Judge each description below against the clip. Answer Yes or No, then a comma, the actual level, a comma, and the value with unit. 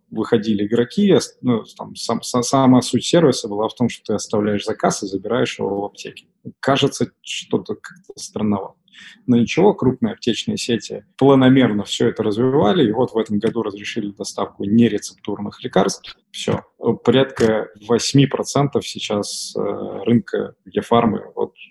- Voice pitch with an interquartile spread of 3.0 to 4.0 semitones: Yes, average, 3.5 semitones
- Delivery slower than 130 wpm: No, average, 140 wpm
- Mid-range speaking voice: No, low, 115 Hz